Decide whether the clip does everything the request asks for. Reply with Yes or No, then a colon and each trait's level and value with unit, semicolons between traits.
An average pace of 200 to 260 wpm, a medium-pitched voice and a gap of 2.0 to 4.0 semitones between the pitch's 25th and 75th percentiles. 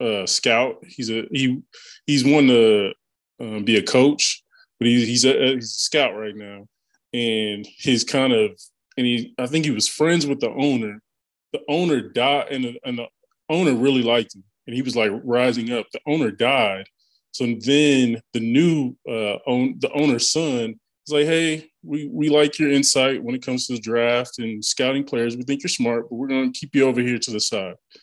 No: fast, 205 wpm; low, 125 Hz; average, 3.4 semitones